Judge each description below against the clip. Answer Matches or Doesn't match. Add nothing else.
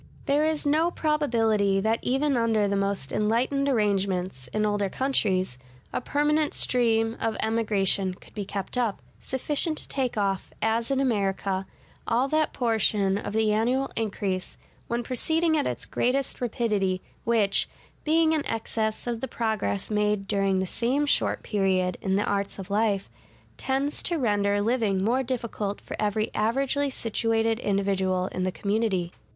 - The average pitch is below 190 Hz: Doesn't match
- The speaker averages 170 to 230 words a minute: Doesn't match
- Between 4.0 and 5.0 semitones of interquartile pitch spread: Matches